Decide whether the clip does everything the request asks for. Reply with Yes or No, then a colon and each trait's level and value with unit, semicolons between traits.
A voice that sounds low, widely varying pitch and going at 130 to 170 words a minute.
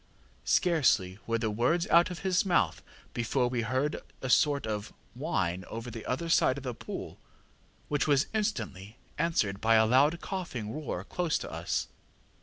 Yes: low, 125 Hz; wide, 6.6 semitones; average, 165 wpm